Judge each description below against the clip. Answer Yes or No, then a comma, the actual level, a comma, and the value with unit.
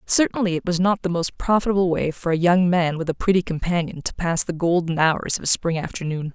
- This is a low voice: No, medium, 175 Hz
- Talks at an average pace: No, fast, 235 wpm